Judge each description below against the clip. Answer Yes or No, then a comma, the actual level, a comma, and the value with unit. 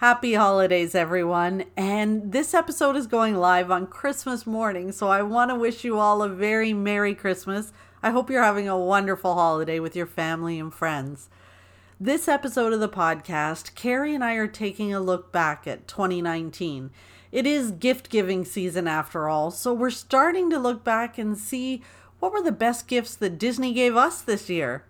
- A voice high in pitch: Yes, high, 205 Hz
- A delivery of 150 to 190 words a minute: Yes, average, 185 wpm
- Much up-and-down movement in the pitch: Yes, wide, 5.7 semitones